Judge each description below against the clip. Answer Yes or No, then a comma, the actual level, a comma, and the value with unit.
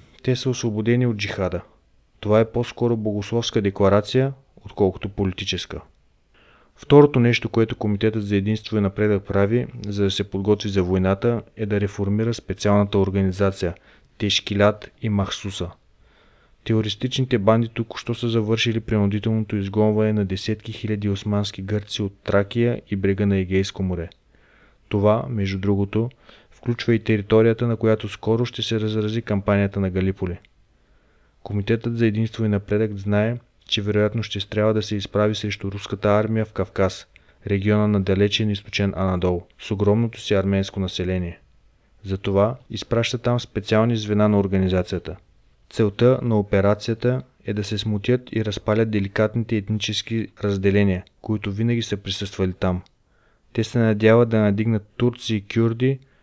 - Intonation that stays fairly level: Yes, narrow, 2.2 semitones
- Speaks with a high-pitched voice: No, low, 105 Hz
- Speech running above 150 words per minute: No, average, 140 wpm